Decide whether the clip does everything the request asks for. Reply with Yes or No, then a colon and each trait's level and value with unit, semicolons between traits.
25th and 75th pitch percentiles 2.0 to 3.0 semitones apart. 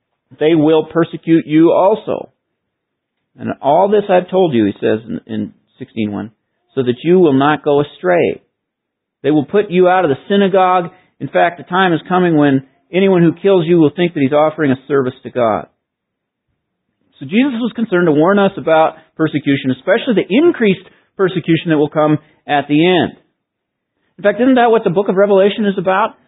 No: average, 4.8 semitones